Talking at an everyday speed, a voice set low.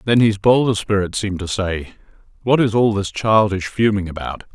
Yes: average, 185 wpm; low, 105 Hz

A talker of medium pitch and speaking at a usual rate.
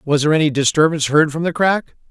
No: medium, 155 Hz; fast, 230 wpm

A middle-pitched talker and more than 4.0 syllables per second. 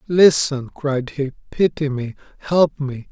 No: medium, 145 Hz; 3.7 syllables/s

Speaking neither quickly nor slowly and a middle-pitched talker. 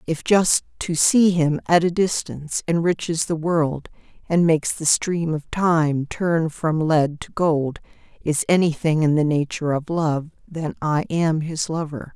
Yes: average, 170 wpm; medium, 160 Hz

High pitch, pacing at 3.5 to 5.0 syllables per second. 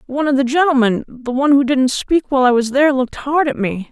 No: very high, 270 Hz; 6.5 syllables/s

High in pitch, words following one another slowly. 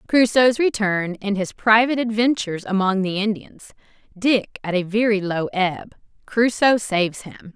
Yes: high, 210 Hz; slow, 125 wpm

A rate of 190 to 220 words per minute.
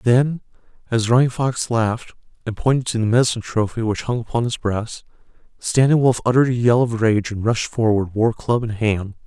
Yes: average, 195 wpm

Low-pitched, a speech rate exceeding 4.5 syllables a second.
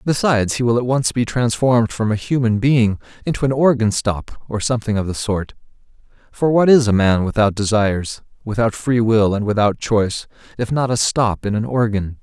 Yes: low, 115 Hz; 5.3 syllables/s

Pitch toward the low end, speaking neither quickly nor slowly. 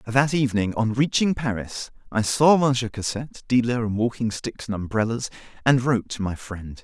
Yes: low, 115 Hz; average, 175 wpm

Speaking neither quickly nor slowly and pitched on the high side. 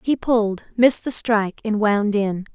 Yes: average, 190 wpm; high, 215 Hz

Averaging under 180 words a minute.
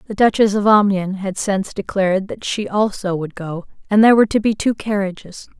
No: fast, 205 wpm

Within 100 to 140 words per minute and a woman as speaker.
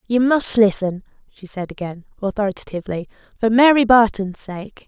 Yes: slow, 135 wpm; female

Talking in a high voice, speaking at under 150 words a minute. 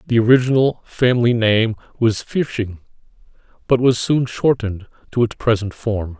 No: low, 115 Hz; slow, 135 wpm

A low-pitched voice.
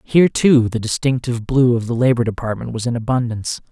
Yes: low, 120 Hz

